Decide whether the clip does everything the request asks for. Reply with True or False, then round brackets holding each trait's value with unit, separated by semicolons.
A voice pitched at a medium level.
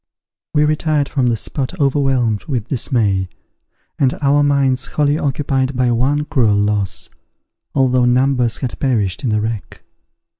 False (130 Hz)